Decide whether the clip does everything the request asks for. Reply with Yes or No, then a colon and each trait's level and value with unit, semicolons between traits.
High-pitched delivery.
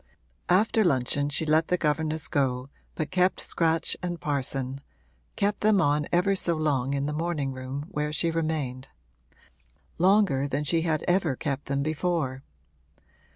No: medium, 155 Hz